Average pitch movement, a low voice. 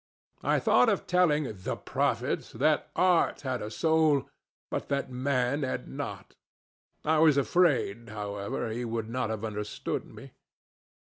No: wide, 5.7 semitones; low, 130 Hz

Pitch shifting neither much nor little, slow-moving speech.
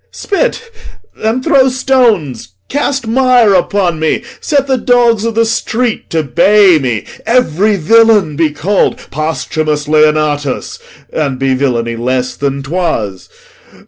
No: wide, 8.0 semitones; slow, 125 wpm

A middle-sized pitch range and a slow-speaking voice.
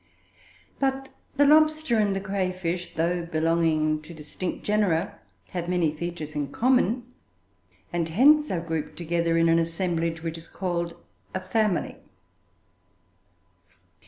Yes: average, 3.8 semitones; slow, 130 wpm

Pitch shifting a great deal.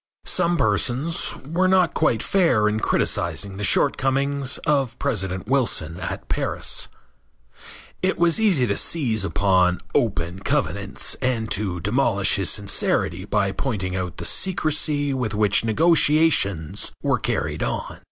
Yes: wide, 6.8 semitones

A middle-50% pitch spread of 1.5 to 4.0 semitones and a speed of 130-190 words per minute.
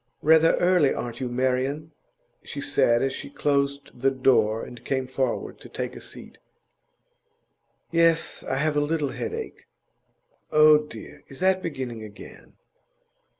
Yes: average, 3.4 semitones; average, 140 wpm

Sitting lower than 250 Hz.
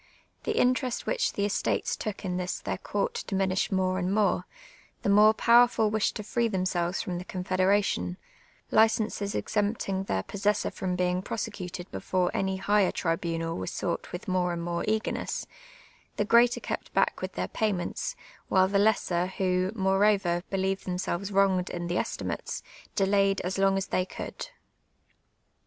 Yes: high, 190 Hz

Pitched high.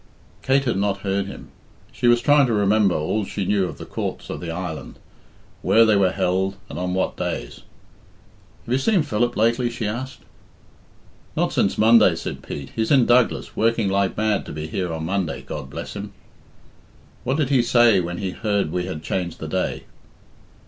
No: low, 100 Hz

